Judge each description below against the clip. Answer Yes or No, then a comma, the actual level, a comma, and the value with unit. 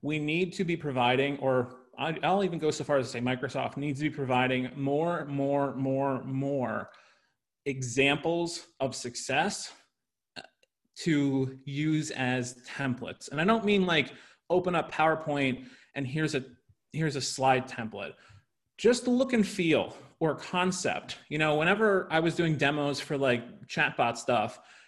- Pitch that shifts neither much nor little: Yes, average, 3.6 semitones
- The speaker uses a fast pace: No, average, 150 wpm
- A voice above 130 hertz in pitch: Yes, medium, 140 Hz